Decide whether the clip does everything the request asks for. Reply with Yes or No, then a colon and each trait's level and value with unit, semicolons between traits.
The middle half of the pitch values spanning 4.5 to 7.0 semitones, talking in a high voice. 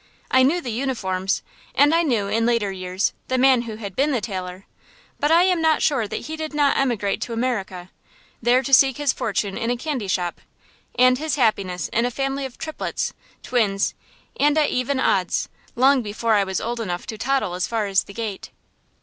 Yes: wide, 5.4 semitones; high, 235 Hz